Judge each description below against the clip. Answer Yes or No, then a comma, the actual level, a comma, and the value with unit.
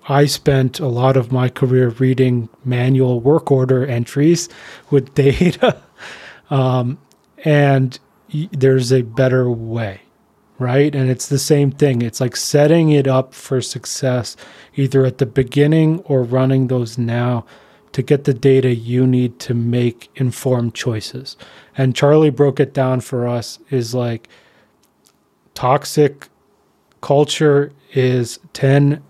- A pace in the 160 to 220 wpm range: No, slow, 135 wpm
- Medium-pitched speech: No, low, 130 Hz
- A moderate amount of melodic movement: No, narrow, 2.2 semitones